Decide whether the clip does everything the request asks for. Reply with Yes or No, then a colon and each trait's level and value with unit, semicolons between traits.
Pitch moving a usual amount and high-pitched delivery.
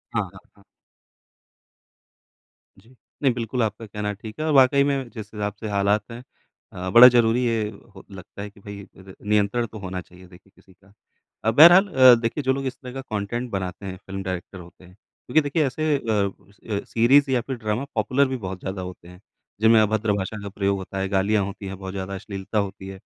No: average, 4.0 semitones; low, 105 Hz